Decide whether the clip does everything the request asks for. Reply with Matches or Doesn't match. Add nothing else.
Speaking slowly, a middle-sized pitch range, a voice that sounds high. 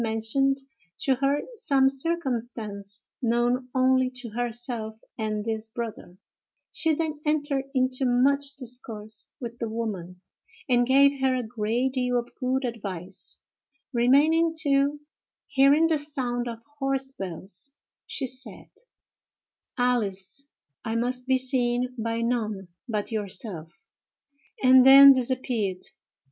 Matches